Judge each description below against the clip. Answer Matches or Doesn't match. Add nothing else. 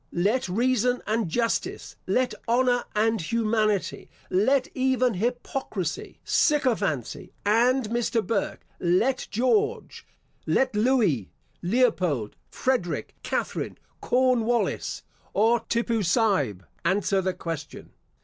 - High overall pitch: Matches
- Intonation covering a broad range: Doesn't match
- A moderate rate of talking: Doesn't match